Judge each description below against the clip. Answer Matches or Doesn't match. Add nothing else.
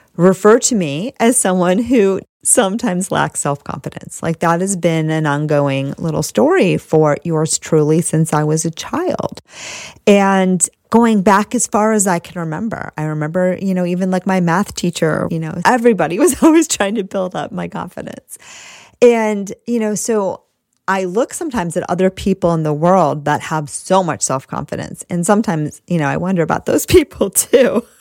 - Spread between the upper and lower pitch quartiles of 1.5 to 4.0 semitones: Doesn't match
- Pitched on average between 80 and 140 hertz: Doesn't match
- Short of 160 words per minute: Doesn't match